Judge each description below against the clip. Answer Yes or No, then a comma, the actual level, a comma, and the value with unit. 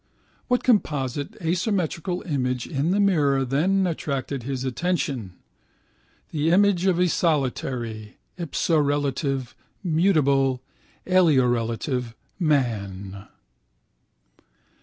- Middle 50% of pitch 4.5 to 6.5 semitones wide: Yes, wide, 5.4 semitones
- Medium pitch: Yes, medium, 145 Hz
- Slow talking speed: Yes, slow, 80 wpm